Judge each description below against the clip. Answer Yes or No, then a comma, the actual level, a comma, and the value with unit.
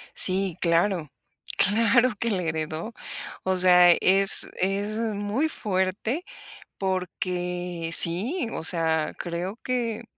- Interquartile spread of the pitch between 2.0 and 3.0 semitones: No, average, 3.5 semitones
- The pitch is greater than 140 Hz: Yes, high, 190 Hz